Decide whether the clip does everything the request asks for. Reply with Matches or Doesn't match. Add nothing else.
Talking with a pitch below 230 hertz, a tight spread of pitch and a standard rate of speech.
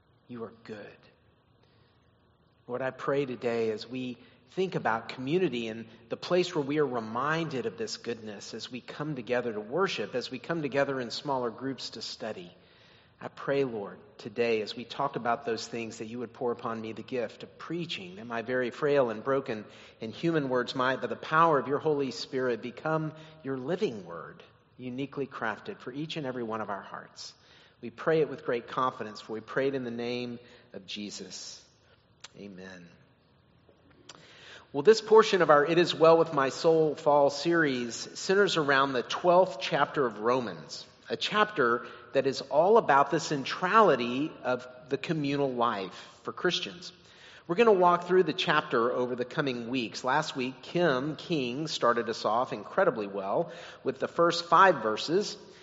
Doesn't match